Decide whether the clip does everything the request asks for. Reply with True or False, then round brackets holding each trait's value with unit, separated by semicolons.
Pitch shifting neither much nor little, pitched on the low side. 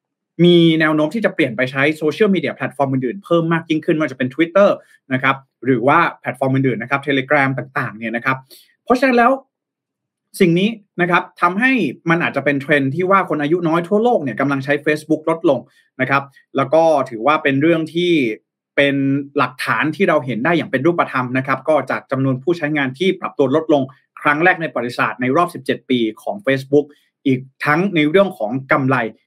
False (4.4 semitones; 150 Hz)